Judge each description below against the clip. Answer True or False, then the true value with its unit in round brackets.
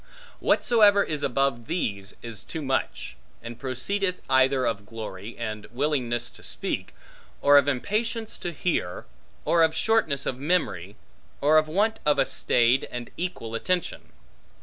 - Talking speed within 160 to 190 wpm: False (145 wpm)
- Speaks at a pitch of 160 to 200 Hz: False (140 Hz)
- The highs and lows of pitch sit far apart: True (7.0 semitones)